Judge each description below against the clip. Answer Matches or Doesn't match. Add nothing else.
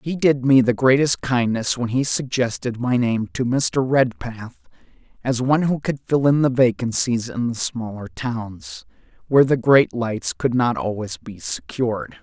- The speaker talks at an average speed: Matches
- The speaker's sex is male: Matches